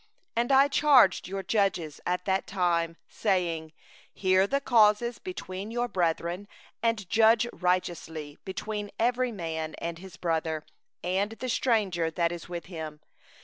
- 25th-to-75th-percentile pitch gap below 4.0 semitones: No, average, 4.8 semitones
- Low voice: No, medium, 185 Hz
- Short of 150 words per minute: Yes, average, 140 wpm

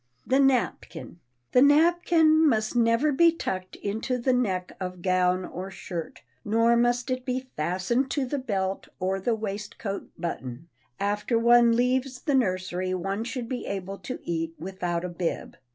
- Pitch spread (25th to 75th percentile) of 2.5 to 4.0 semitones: No, wide, 5.4 semitones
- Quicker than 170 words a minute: No, average, 160 wpm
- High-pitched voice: Yes, high, 220 Hz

